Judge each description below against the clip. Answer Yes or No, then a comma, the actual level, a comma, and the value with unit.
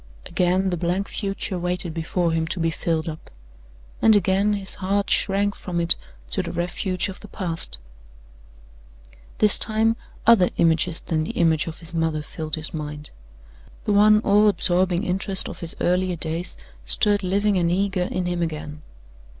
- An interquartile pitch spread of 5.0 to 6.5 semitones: No, average, 3.2 semitones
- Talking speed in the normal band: Yes, average, 165 wpm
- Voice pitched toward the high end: No, medium, 180 Hz